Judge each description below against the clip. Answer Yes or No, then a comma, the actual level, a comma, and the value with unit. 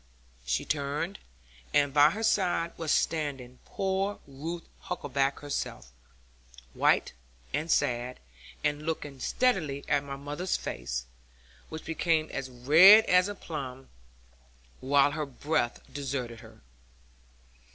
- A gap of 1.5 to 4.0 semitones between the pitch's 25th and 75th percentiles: Yes, average, 3.5 semitones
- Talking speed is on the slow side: Yes, slow, 115 wpm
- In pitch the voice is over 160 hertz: No, medium, 145 Hz